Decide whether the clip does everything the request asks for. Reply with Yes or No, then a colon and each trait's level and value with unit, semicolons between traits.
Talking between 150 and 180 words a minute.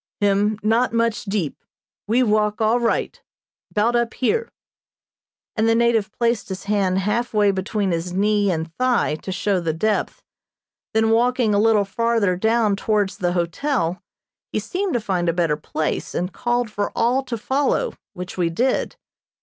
Yes: average, 165 wpm